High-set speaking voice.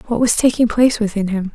Yes: high, 220 Hz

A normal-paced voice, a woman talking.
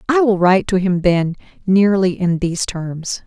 Yes: average, 185 wpm; female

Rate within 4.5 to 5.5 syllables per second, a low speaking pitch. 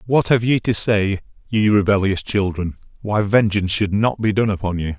Yes: 5.1 syllables/s; low, 100 Hz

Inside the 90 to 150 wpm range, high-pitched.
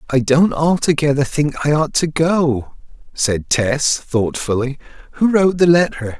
No: average, 145 wpm; medium, 145 Hz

